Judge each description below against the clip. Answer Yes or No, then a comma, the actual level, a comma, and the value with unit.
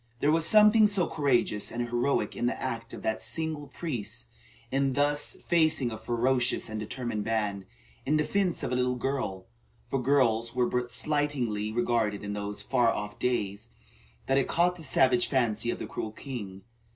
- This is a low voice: Yes, low, 125 Hz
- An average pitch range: Yes, average, 4.7 semitones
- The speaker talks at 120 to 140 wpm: No, average, 175 wpm